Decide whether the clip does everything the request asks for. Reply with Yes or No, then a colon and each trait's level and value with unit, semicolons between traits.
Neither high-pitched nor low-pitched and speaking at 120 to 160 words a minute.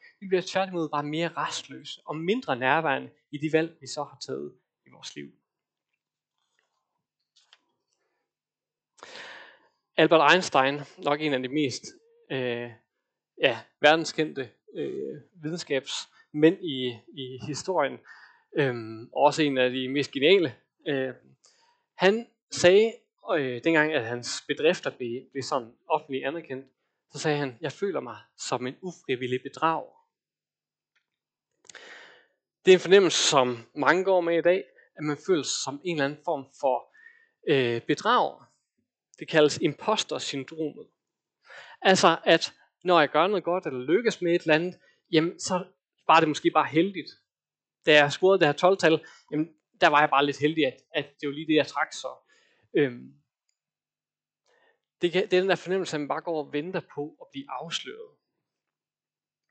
Yes: medium, 155 Hz; slow, 145 wpm